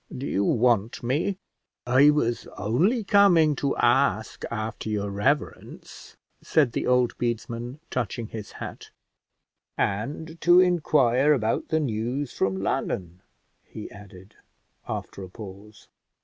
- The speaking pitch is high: No, low, 120 Hz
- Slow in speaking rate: Yes, slow, 120 wpm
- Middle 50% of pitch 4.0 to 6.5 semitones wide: Yes, wide, 5.6 semitones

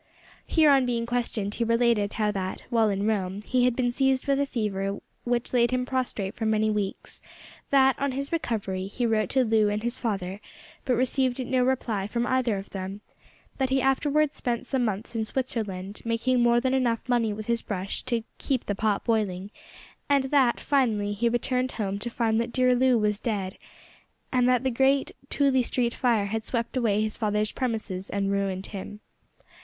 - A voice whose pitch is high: Yes, high, 235 Hz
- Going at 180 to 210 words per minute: Yes, average, 190 wpm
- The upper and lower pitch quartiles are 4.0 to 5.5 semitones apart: No, average, 3.5 semitones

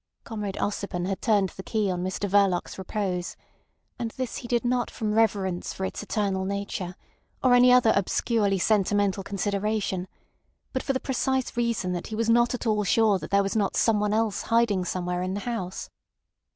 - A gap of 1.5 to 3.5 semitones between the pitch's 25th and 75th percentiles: Yes, average, 3.1 semitones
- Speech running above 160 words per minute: Yes, average, 180 wpm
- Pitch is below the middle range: No, high, 205 Hz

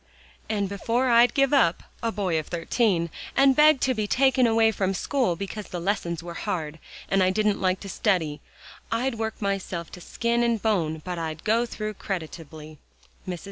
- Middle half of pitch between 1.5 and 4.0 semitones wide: No, average, 5.3 semitones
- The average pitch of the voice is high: Yes, high, 200 Hz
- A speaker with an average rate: Yes, average, 180 wpm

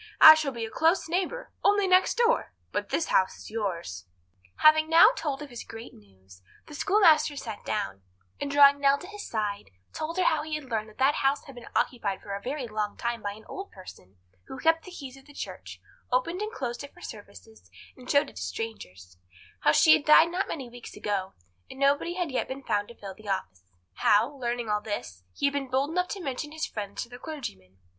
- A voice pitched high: Yes, very high, 260 Hz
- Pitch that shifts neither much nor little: No, wide, 7.2 semitones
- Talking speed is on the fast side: Yes, fast, 220 wpm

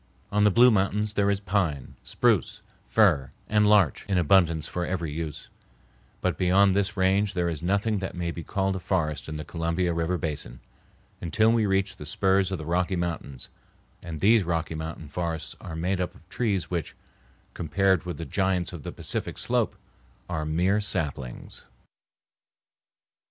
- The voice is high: No, very low, 90 Hz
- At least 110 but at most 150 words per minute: No, average, 165 wpm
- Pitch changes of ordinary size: Yes, average, 3.3 semitones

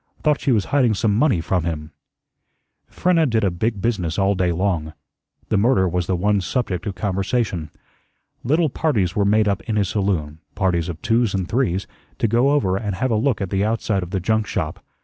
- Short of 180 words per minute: No, fast, 205 wpm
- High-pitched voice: No, low, 100 Hz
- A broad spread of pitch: No, average, 4.1 semitones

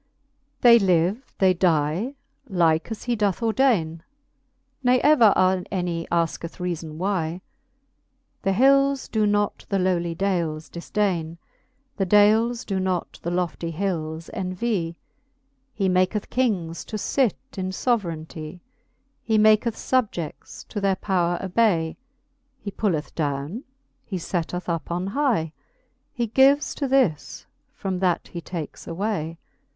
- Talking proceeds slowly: Yes, slow, 125 wpm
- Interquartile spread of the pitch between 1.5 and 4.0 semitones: No, average, 4.7 semitones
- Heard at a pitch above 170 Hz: Yes, medium, 185 Hz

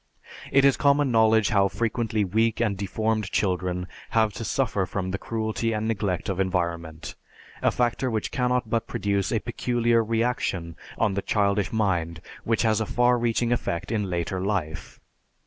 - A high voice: No, low, 110 Hz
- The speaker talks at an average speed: Yes, average, 165 wpm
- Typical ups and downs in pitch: Yes, average, 3.4 semitones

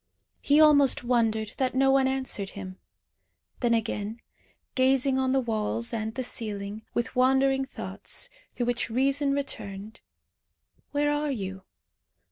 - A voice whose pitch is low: No, very high, 255 Hz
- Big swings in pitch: No, average, 3.6 semitones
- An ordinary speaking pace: No, slow, 130 wpm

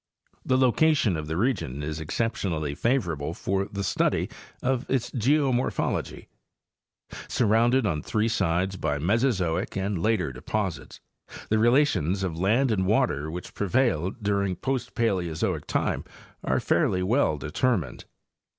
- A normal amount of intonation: No, wide, 6.3 semitones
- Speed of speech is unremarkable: No, slow, 125 wpm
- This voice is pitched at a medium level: No, low, 100 Hz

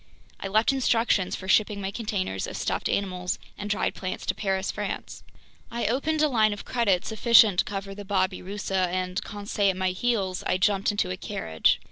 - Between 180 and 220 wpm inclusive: Yes, average, 185 wpm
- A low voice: No, high, 200 Hz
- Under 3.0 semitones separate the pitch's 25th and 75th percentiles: Yes, narrow, 2.6 semitones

